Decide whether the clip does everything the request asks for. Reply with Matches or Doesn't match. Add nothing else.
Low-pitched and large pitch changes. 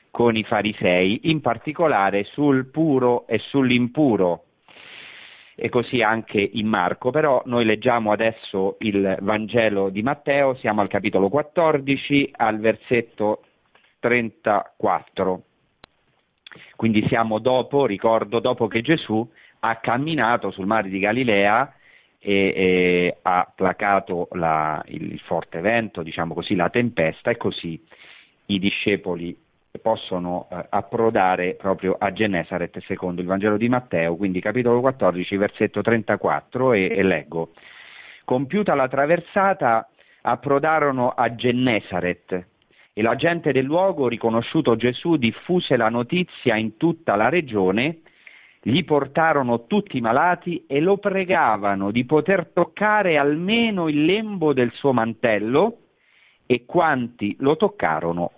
Matches